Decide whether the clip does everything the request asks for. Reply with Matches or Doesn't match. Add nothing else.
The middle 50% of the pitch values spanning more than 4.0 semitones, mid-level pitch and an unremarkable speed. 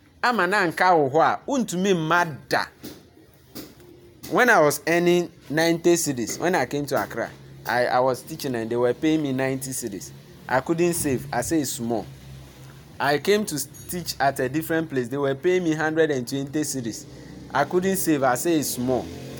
Matches